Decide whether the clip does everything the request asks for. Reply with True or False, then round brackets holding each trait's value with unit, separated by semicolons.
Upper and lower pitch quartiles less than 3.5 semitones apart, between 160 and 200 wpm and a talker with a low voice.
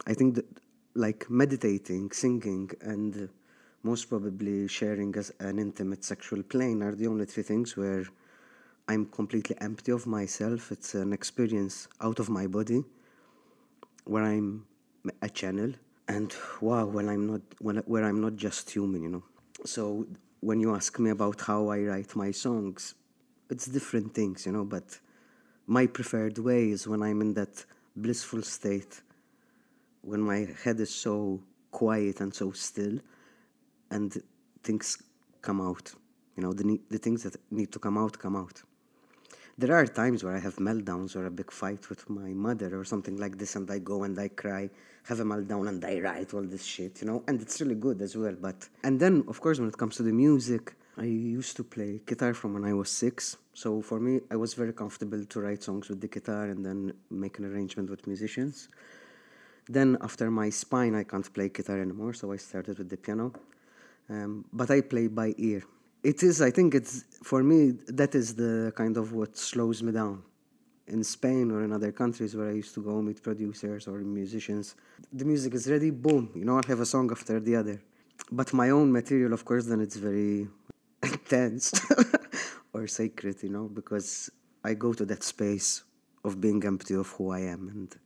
True (2.8 semitones; 190 wpm; 105 Hz)